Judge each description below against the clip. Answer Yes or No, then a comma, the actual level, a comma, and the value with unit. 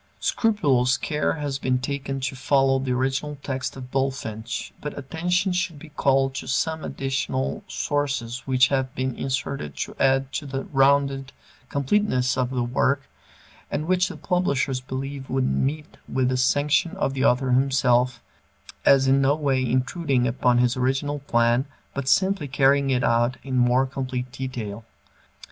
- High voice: No, low, 135 Hz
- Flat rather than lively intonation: Yes, narrow, 1.8 semitones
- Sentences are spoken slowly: No, average, 155 wpm